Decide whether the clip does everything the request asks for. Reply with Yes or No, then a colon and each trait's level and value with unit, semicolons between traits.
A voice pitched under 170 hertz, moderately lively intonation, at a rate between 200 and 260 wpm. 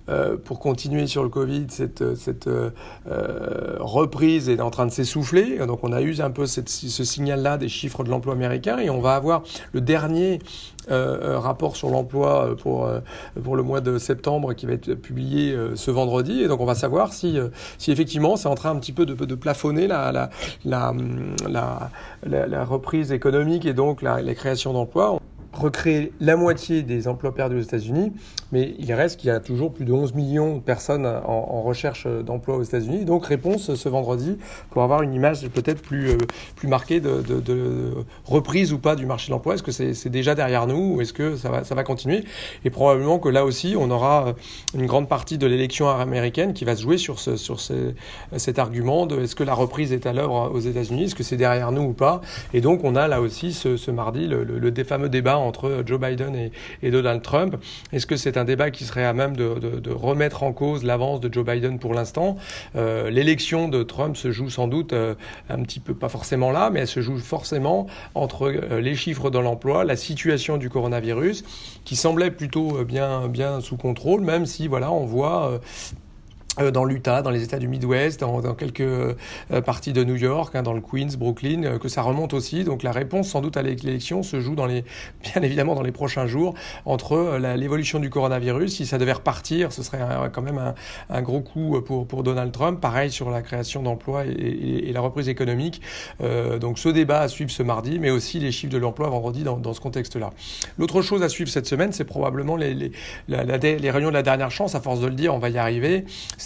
Yes: low, 135 Hz; average, 3.3 semitones; fast, 220 wpm